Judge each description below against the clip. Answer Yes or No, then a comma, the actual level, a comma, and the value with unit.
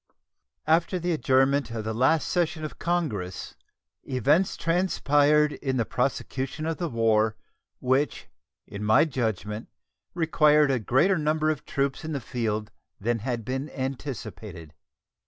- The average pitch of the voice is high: No, low, 135 Hz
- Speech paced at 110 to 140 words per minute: Yes, slow, 135 wpm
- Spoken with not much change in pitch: No, average, 5.1 semitones